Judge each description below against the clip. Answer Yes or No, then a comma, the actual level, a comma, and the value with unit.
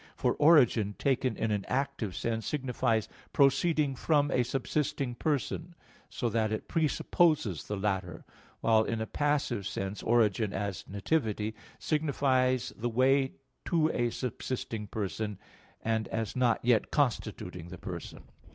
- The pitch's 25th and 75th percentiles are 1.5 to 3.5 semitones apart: No, average, 4.7 semitones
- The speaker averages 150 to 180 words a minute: No, slow, 135 wpm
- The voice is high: No, low, 120 Hz